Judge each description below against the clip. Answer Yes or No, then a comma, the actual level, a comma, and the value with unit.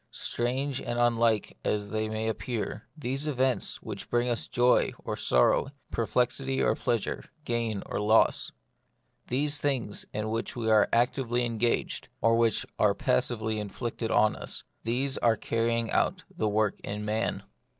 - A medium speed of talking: Yes, average, 160 wpm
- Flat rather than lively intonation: Yes, narrow, 2.2 semitones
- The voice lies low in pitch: Yes, low, 115 Hz